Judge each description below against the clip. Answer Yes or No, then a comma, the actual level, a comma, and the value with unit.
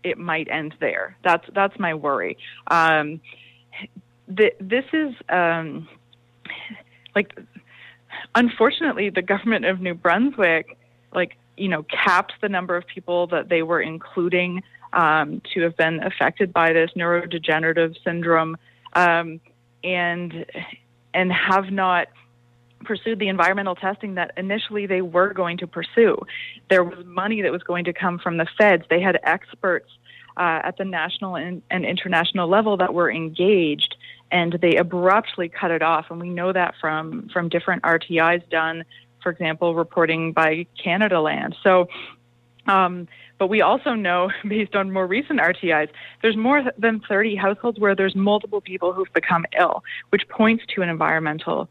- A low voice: No, medium, 180 Hz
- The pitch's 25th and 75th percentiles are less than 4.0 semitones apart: Yes, average, 3.2 semitones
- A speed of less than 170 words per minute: Yes, average, 150 wpm